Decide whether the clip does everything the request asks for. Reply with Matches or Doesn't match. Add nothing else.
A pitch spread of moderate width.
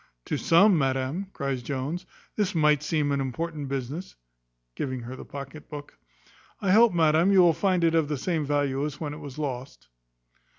Matches